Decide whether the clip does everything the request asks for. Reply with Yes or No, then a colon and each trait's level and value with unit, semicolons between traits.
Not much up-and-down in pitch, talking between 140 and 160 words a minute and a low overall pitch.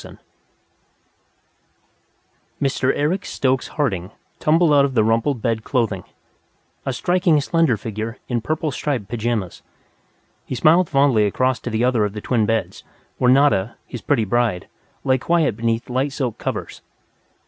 No: average, 4.2 semitones; average, 145 wpm; low, 125 Hz